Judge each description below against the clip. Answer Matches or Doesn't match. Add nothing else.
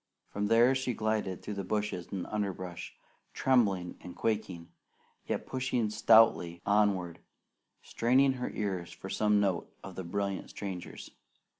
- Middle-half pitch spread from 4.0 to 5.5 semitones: Doesn't match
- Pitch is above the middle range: Doesn't match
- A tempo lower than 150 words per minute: Matches